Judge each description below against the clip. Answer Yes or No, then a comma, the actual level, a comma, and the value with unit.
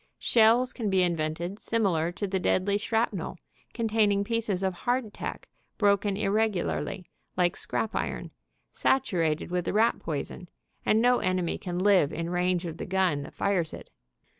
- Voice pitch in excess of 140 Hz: Yes, high, 190 Hz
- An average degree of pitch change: Yes, average, 3.6 semitones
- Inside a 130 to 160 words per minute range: Yes, average, 155 wpm